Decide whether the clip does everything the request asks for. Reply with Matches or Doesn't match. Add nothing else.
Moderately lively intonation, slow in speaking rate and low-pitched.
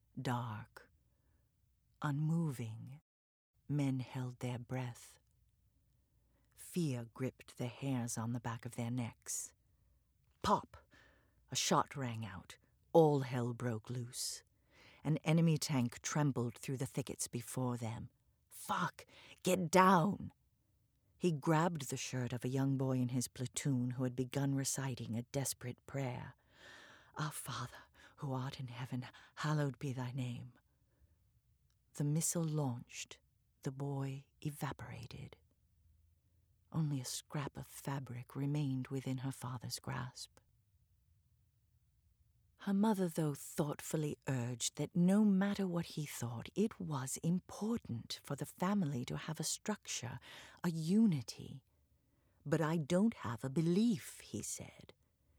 Matches